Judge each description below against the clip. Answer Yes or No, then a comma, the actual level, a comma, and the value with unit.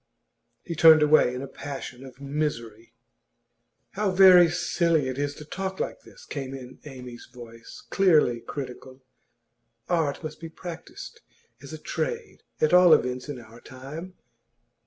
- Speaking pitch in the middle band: Yes, medium, 145 Hz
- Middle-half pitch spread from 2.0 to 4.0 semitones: No, average, 4.9 semitones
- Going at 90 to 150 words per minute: Yes, average, 145 wpm